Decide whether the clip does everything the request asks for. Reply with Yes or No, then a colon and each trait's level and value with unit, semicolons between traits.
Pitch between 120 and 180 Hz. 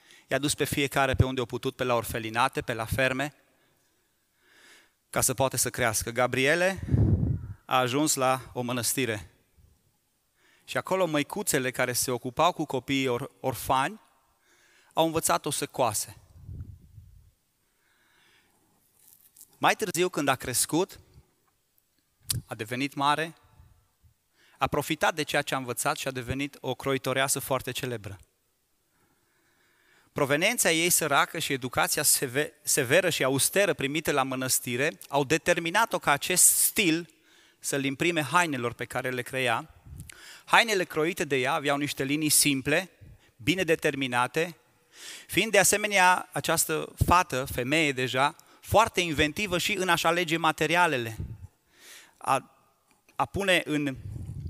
Yes: low, 135 Hz